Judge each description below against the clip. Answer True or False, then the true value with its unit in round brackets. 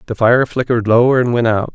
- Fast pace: True (240 wpm)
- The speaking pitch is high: False (120 Hz)